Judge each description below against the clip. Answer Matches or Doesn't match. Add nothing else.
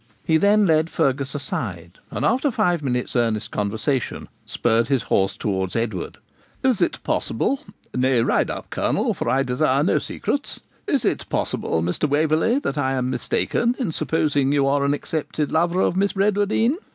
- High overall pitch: Doesn't match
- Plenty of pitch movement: Matches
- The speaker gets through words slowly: Doesn't match